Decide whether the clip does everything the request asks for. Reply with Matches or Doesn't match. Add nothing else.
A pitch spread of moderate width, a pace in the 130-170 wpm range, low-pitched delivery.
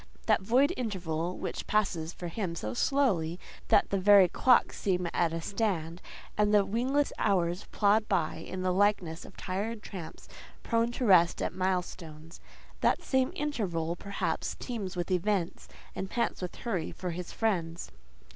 Doesn't match